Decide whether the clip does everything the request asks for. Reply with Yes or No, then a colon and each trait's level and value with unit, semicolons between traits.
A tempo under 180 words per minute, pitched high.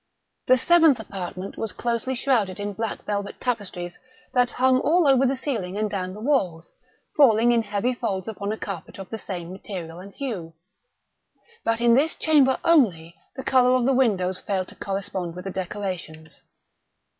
Yes: average, 170 wpm; high, 210 Hz